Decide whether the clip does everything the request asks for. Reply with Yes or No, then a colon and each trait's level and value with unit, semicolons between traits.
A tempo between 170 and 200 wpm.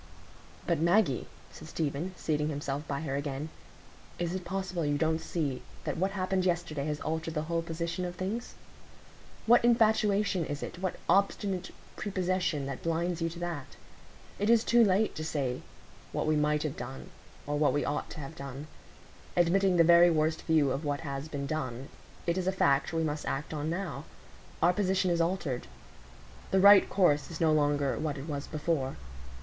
Yes: average, 180 wpm